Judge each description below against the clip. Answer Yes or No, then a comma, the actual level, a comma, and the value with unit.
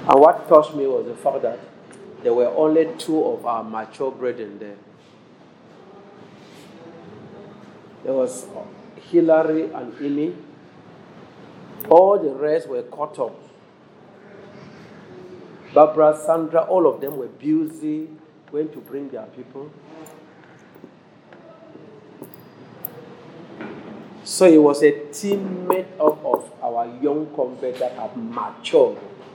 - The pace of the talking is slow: Yes, slow, 110 wpm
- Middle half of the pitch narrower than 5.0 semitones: No, wide, 5.6 semitones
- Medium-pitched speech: Yes, medium, 160 Hz